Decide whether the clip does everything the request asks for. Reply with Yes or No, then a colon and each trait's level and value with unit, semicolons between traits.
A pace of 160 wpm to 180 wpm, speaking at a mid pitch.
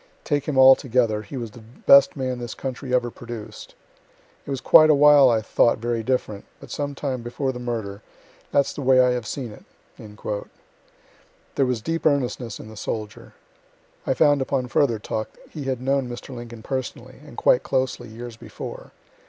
No: average, 175 wpm; low, 125 Hz